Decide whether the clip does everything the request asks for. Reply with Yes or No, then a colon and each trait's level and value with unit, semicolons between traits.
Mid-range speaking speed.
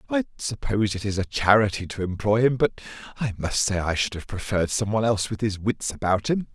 No: fast, 220 wpm